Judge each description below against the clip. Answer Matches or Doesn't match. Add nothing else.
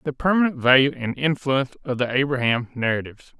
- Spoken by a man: Matches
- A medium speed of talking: Matches